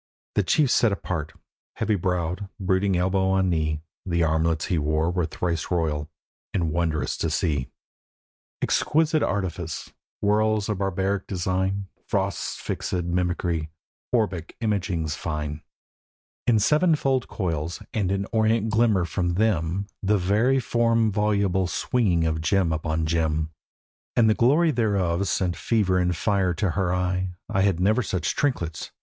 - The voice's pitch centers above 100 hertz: No, very low, 95 Hz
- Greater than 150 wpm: No, slow, 135 wpm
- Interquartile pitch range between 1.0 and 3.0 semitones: No, average, 4.0 semitones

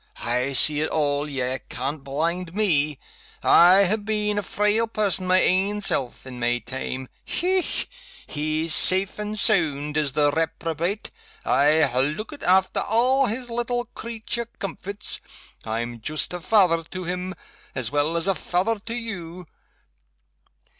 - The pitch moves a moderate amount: No, wide, 6.2 semitones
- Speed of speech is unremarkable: Yes, average, 145 wpm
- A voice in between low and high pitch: Yes, medium, 175 Hz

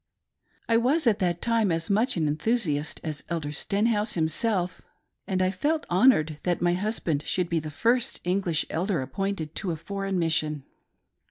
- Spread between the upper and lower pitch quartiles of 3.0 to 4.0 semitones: No, average, 5.2 semitones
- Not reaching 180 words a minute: Yes, average, 170 wpm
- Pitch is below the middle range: No, medium, 185 Hz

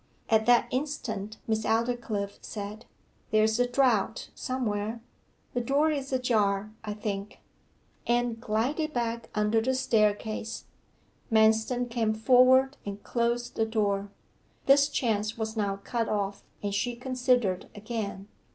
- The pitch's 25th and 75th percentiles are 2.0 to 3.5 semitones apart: Yes, average, 2.8 semitones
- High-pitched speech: Yes, high, 225 Hz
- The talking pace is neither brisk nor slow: No, slow, 125 wpm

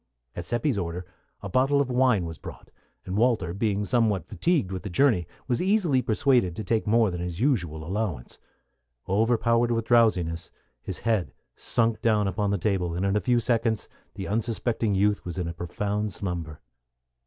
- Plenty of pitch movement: No, average, 4.7 semitones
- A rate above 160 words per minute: Yes, average, 175 wpm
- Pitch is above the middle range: No, low, 105 Hz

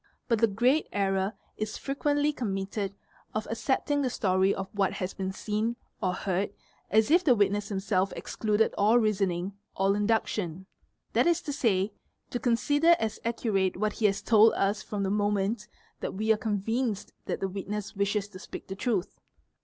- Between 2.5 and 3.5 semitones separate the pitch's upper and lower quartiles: Yes, average, 2.8 semitones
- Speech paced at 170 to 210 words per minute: Yes, average, 175 wpm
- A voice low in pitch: No, high, 210 Hz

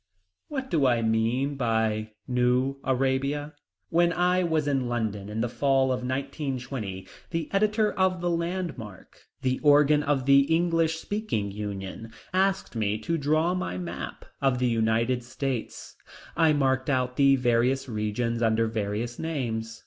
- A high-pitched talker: No, low, 130 Hz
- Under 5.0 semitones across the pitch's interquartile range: No, wide, 5.5 semitones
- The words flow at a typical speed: Yes, average, 145 wpm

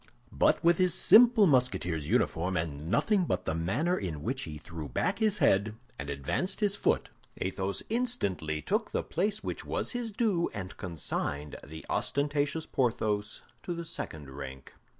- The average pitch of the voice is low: Yes, low, 105 Hz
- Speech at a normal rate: Yes, average, 160 wpm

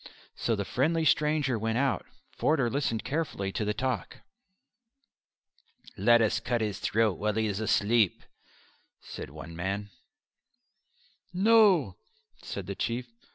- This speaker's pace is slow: Yes, slow, 125 wpm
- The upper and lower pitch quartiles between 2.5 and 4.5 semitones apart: No, average, 4.9 semitones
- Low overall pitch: Yes, low, 115 Hz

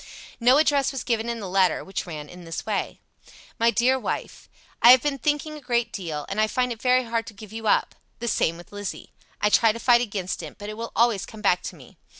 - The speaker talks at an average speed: No, fast, 245 wpm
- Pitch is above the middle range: Yes, high, 230 Hz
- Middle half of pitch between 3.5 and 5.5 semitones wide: Yes, average, 3.9 semitones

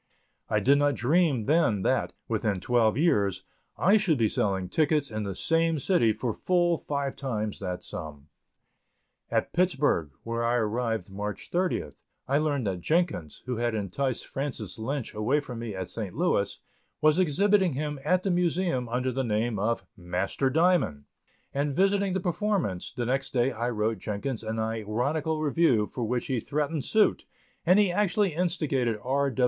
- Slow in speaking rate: No, average, 165 wpm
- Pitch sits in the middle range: No, low, 130 Hz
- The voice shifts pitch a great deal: Yes, wide, 6.9 semitones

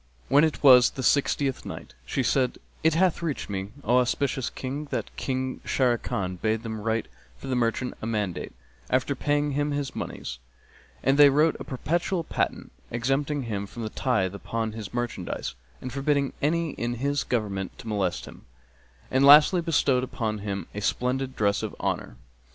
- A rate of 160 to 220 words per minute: Yes, average, 170 wpm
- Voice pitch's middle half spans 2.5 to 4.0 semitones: No, average, 4.4 semitones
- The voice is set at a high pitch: No, low, 130 Hz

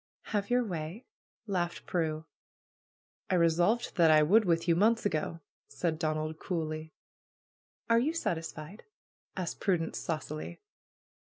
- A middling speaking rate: No, slow, 120 wpm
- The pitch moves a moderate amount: Yes, average, 4.3 semitones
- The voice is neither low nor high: Yes, medium, 170 Hz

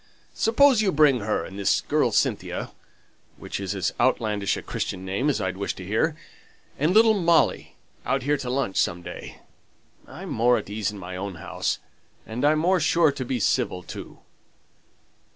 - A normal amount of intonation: No, wide, 7.8 semitones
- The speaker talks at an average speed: Yes, average, 180 wpm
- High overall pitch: No, low, 120 Hz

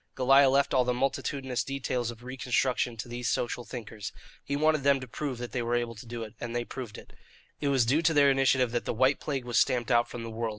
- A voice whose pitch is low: Yes, low, 125 Hz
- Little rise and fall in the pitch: Yes, narrow, 2.3 semitones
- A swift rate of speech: Yes, fast, 250 wpm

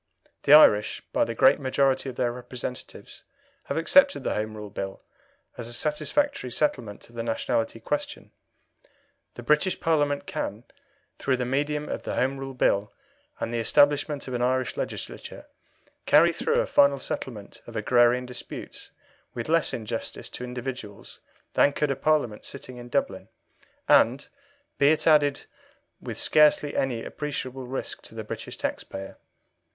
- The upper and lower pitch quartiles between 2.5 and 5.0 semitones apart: Yes, average, 3.7 semitones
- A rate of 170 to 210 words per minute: No, average, 150 wpm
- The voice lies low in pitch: Yes, low, 130 Hz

